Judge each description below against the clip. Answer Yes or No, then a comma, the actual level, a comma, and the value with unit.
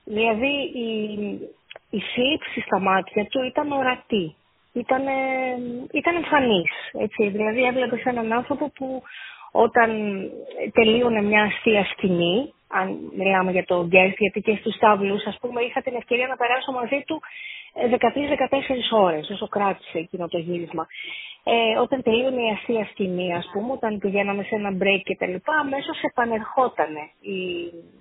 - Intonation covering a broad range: No, average, 4.6 semitones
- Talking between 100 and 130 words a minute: No, average, 140 wpm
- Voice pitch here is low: No, high, 230 Hz